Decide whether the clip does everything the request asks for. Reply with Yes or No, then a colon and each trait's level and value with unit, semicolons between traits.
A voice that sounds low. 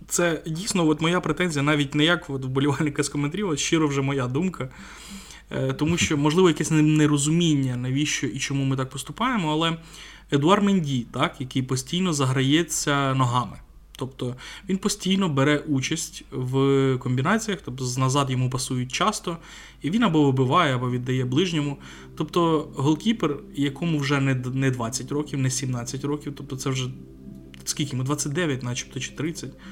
No: medium, 145 Hz